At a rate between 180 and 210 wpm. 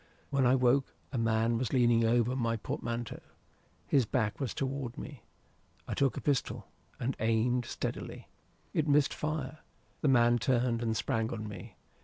No: average, 160 wpm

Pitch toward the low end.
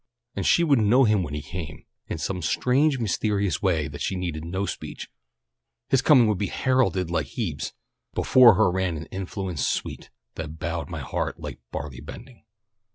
Yes: very low, 95 Hz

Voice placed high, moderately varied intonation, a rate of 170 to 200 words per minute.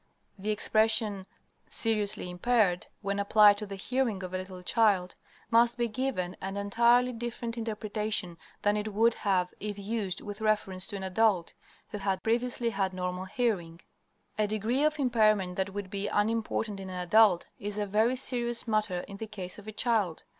Yes: high, 210 Hz; average, 3.0 semitones; average, 175 wpm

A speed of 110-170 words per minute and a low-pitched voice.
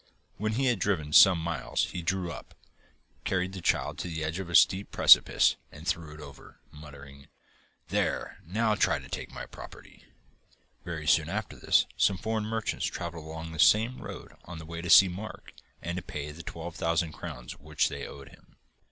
No: average, 190 wpm; very low, 85 Hz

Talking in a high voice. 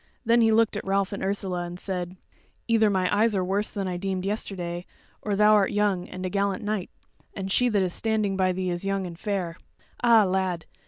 Yes: high, 195 Hz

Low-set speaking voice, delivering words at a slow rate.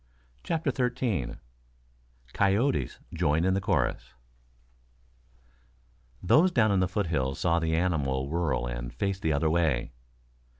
Yes: very low, 85 Hz; slow, 120 wpm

